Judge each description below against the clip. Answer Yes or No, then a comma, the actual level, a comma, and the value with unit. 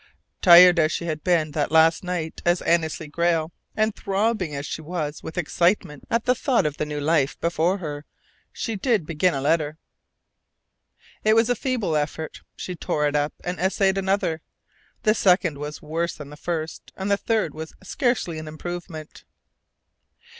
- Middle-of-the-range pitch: Yes, medium, 170 Hz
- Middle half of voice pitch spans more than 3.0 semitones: Yes, average, 3.7 semitones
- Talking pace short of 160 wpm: No, average, 170 wpm